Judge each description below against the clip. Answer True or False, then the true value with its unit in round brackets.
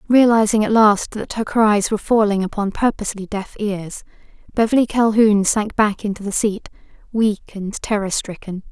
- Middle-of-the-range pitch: False (210 Hz)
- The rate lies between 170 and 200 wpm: False (160 wpm)